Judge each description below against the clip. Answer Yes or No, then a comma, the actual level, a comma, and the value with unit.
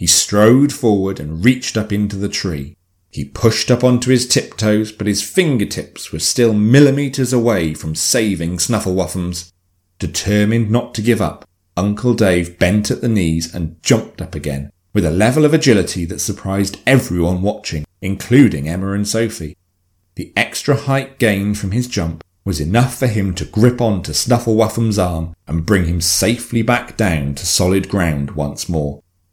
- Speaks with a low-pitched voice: Yes, low, 100 Hz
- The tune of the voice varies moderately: Yes, average, 4.5 semitones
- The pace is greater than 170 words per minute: No, average, 165 wpm